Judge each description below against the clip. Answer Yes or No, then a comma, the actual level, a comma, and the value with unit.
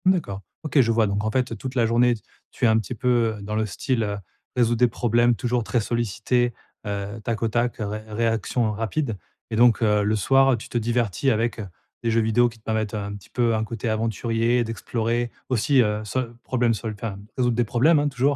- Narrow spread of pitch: Yes, narrow, 2.0 semitones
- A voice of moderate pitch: No, low, 115 Hz